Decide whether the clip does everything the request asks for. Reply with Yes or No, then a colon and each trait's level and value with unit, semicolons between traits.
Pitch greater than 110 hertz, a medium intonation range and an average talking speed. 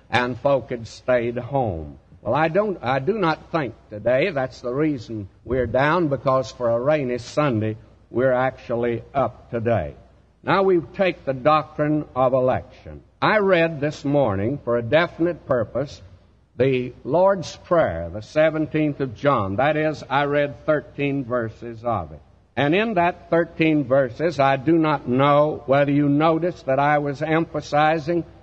Yes: medium, 140 Hz; average, 4.6 semitones; average, 155 wpm